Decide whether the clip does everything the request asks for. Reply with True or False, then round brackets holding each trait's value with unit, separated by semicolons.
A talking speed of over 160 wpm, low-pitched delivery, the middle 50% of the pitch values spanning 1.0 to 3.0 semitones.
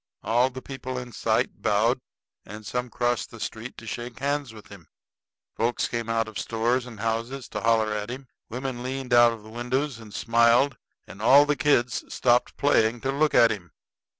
True (185 wpm; 120 Hz; 2.4 semitones)